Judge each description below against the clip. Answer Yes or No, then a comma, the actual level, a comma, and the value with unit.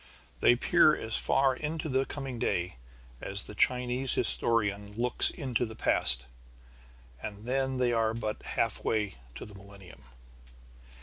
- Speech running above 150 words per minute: No, slow, 135 wpm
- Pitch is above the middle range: No, low, 115 Hz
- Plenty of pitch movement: No, average, 4.1 semitones